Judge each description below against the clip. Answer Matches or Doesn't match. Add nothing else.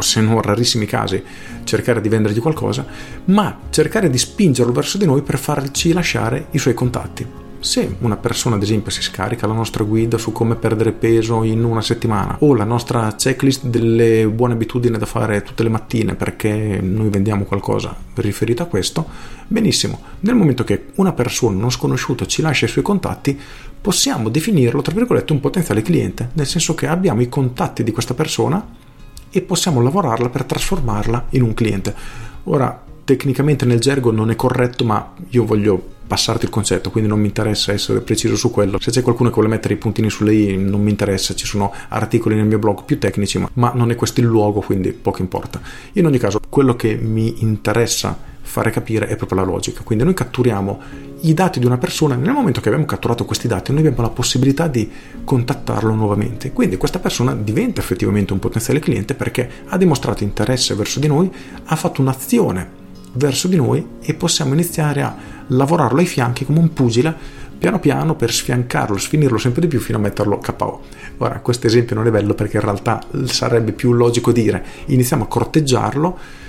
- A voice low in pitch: Matches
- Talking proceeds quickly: Matches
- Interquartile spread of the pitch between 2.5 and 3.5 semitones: Doesn't match